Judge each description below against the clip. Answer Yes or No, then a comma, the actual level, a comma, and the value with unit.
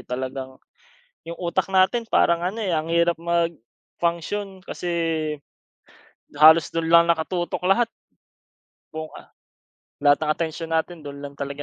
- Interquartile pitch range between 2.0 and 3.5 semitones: Yes, narrow, 2.5 semitones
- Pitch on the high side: No, medium, 170 Hz